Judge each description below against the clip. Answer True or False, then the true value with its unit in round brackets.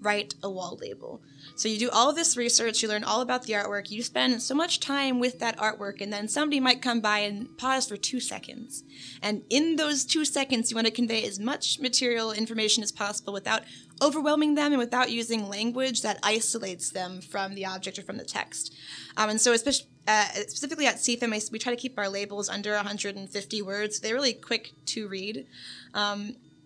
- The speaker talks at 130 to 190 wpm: False (205 wpm)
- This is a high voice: True (220 Hz)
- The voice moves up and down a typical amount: True (3.6 semitones)